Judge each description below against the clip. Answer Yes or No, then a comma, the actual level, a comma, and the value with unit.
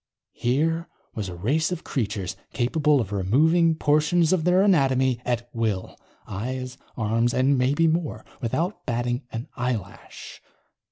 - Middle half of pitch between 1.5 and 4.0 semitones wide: No, wide, 5.6 semitones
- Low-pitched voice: Yes, low, 130 Hz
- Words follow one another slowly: Yes, slow, 130 wpm